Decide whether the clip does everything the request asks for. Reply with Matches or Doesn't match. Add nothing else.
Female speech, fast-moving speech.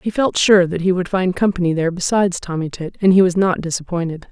Matches